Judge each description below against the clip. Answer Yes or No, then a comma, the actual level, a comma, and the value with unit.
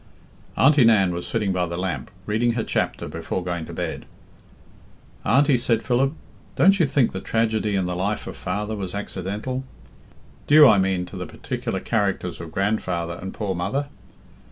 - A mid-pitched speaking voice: No, low, 100 Hz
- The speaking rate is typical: Yes, average, 170 wpm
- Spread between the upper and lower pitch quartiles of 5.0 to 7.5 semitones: No, average, 4.5 semitones